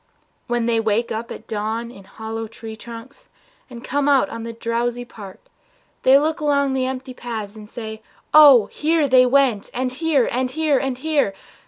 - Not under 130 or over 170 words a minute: No, average, 180 wpm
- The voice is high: Yes, high, 245 Hz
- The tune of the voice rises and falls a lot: No, average, 3.5 semitones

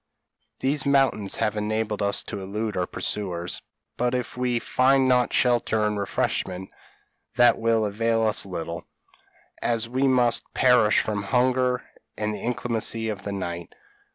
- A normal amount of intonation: Yes, average, 3.4 semitones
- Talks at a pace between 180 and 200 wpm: No, average, 145 wpm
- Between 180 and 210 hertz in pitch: No, low, 110 Hz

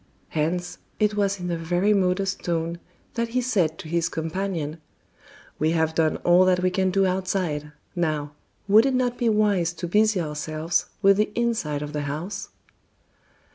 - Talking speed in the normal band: Yes, average, 170 wpm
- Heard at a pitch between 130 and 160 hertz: No, medium, 180 Hz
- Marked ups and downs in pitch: No, average, 3.7 semitones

